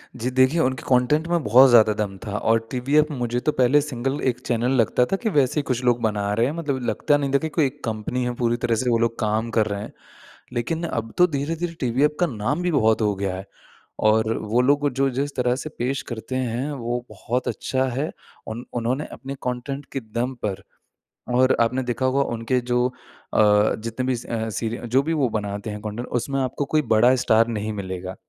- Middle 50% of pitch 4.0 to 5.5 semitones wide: No, average, 3.5 semitones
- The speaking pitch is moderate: No, low, 125 Hz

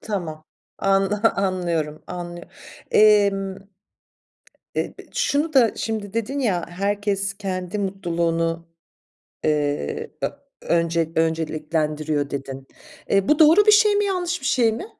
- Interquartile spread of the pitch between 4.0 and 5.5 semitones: Yes, average, 5.1 semitones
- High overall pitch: Yes, high, 195 Hz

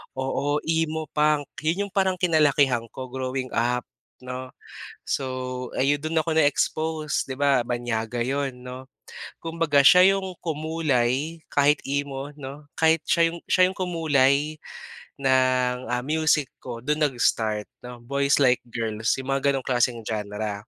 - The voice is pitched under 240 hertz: Yes, medium, 140 Hz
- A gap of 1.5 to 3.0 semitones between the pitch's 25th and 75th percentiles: No, average, 3.7 semitones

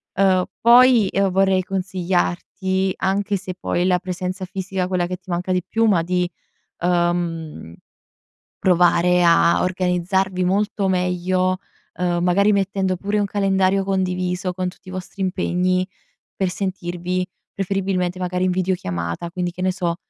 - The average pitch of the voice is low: No, medium, 185 Hz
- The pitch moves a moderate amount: No, narrow, 1.2 semitones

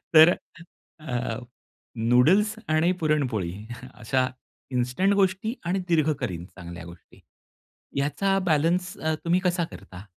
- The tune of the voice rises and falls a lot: Yes, wide, 7.1 semitones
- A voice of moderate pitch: Yes, medium, 150 Hz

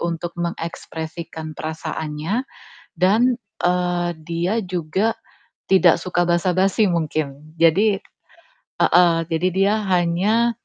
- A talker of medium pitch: Yes, medium, 175 Hz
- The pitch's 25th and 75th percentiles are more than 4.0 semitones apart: No, average, 2.8 semitones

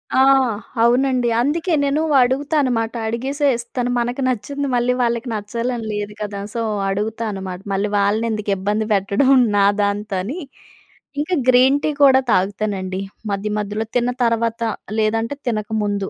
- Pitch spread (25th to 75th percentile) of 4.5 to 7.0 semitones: No, average, 3.6 semitones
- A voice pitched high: Yes, high, 230 Hz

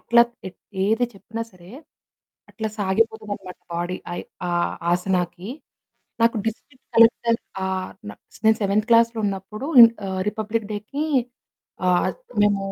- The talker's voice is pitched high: Yes, high, 210 Hz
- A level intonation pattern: No, average, 3.3 semitones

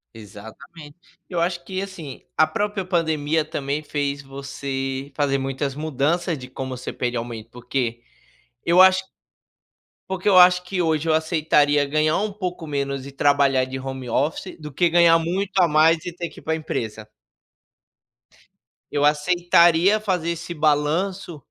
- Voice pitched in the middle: Yes, medium, 155 Hz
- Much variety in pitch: No, average, 4.0 semitones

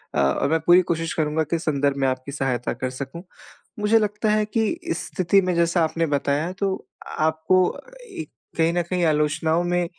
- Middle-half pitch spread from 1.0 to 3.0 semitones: No, average, 3.9 semitones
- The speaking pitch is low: No, medium, 165 Hz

